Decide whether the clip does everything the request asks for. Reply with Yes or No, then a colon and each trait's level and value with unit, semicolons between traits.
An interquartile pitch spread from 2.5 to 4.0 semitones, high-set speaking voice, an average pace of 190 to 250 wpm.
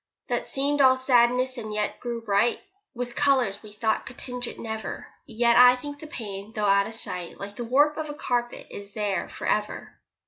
Yes: average, 3.4 semitones; high, 235 Hz; fast, 205 wpm